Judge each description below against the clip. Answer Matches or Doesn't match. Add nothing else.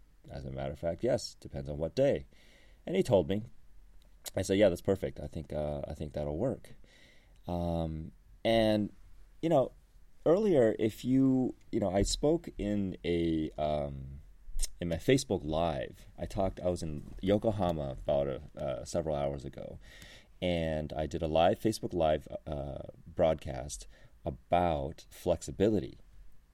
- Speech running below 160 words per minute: Matches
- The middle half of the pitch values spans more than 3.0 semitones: Matches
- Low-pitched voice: Matches